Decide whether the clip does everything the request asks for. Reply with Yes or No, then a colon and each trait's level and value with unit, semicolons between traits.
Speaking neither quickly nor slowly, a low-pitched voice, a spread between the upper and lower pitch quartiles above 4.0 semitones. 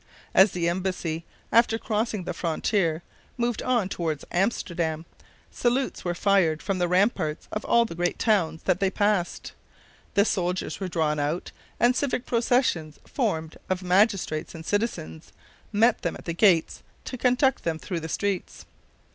No: average, 155 wpm; medium, 185 Hz; average, 4.8 semitones